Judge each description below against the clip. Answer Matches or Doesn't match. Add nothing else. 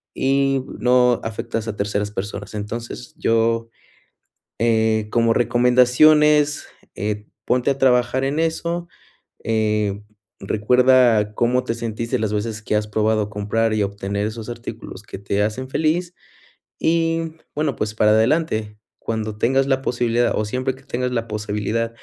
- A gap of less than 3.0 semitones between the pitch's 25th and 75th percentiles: Doesn't match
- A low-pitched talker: Matches